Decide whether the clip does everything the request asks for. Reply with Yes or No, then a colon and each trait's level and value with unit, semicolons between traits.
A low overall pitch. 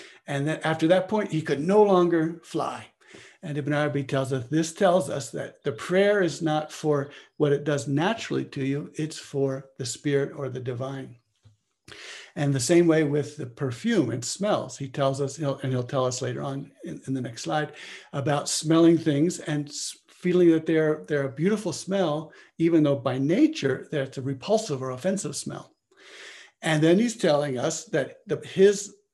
No: medium, 150 Hz